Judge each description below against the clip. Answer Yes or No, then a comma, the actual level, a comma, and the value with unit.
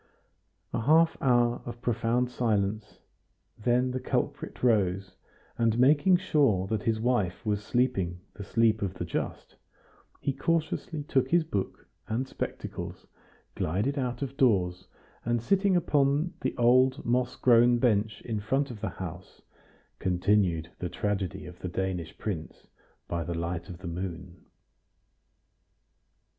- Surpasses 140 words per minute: No, slow, 135 wpm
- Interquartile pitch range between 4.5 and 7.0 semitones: Yes, wide, 5.4 semitones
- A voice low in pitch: Yes, low, 115 Hz